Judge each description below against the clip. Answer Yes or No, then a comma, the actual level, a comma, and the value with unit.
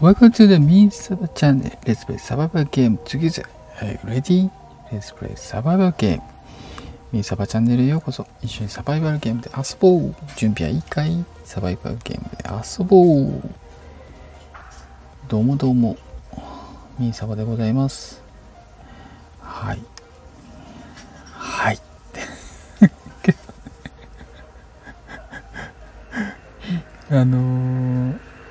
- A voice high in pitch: No, low, 125 Hz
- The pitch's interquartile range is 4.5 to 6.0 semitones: No, wide, 6.7 semitones